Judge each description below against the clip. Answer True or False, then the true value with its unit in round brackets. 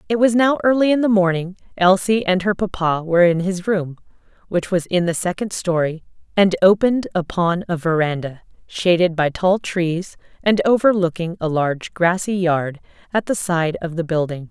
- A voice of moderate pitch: True (180 Hz)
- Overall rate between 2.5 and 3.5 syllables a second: False (5.0 syllables/s)